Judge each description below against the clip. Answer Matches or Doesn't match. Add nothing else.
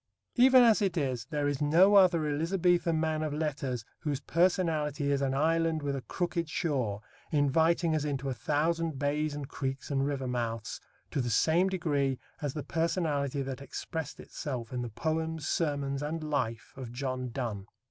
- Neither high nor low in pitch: Matches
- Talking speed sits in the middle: Matches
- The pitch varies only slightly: Doesn't match